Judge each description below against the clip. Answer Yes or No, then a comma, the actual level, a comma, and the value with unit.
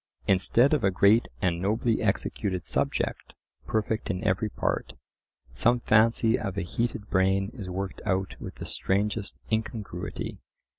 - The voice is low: Yes, low, 100 Hz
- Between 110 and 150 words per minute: Yes, average, 140 wpm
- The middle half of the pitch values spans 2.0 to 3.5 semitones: Yes, average, 3.0 semitones